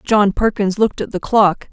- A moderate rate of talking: No, fast, 210 wpm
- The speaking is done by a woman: Yes, female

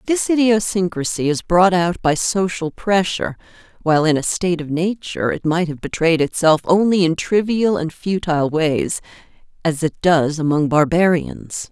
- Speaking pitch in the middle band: Yes, medium, 170 Hz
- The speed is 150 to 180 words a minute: Yes, average, 155 wpm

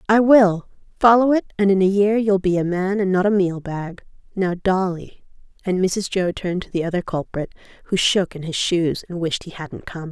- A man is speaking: No, female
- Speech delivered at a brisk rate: Yes, fast, 220 wpm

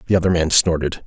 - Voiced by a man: Yes, male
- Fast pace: Yes, fast, 225 wpm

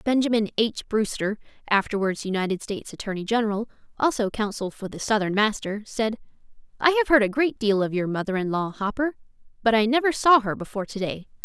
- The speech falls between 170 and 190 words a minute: Yes, average, 185 wpm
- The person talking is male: No, female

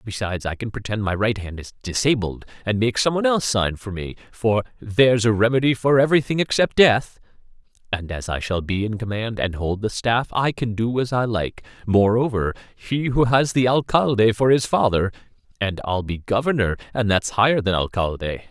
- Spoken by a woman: No, male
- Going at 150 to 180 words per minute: No, average, 195 wpm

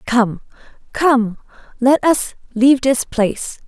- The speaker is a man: No, female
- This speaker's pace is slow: Yes, slow, 115 wpm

